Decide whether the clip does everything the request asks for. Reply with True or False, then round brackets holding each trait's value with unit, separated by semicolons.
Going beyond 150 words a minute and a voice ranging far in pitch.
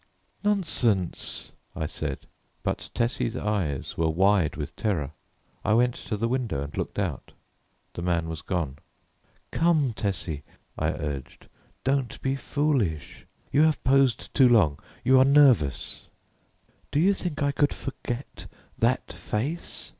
False (135 wpm; 8.8 semitones)